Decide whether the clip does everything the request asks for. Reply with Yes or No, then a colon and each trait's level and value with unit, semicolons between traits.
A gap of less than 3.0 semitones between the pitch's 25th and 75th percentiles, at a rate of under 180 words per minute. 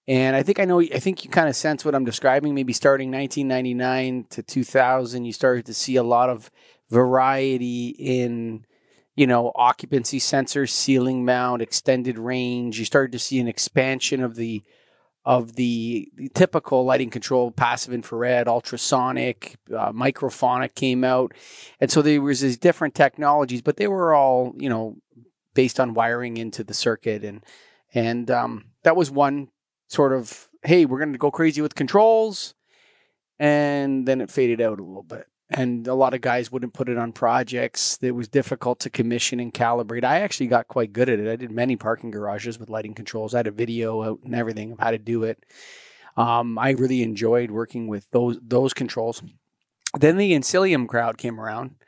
No: narrow, 2.4 semitones; average, 185 wpm